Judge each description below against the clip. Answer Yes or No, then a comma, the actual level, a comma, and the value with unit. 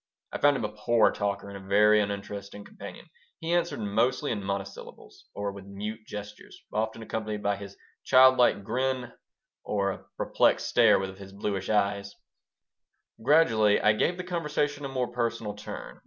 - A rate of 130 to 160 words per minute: No, average, 170 wpm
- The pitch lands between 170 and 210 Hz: No, low, 105 Hz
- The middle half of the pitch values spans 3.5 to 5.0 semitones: Yes, average, 3.9 semitones